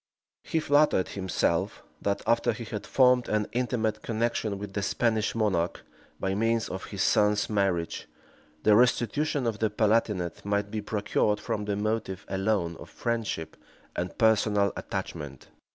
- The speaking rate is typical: Yes, average, 145 wpm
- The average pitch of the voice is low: Yes, low, 105 Hz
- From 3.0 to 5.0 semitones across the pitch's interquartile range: No, narrow, 2.5 semitones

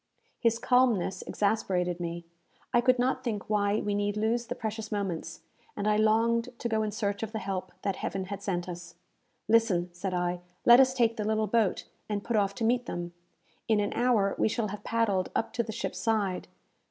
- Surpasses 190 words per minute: Yes, average, 200 wpm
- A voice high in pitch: Yes, high, 210 Hz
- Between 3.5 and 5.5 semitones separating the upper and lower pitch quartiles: No, average, 3.0 semitones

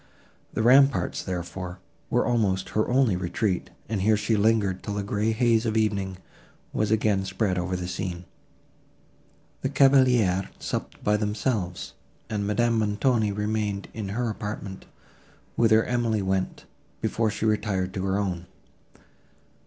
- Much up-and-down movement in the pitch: No, average, 2.8 semitones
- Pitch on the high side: No, low, 105 Hz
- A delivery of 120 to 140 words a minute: Yes, slow, 135 wpm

